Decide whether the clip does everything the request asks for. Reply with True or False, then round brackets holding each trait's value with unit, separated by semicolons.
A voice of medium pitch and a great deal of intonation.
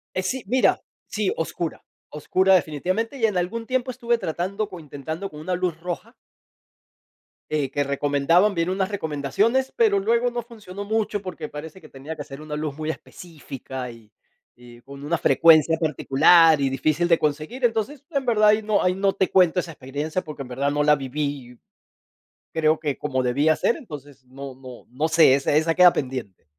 True (160 Hz; 5.7 semitones)